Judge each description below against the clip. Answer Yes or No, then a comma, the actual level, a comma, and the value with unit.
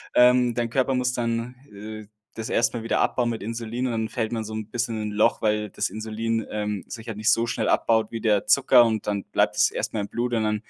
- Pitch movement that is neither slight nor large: No, narrow, 1.8 semitones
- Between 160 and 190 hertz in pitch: No, low, 115 Hz